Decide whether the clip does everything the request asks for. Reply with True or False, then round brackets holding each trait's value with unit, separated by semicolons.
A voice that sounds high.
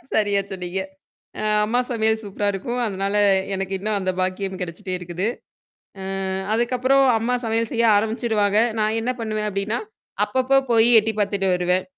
True (210 Hz)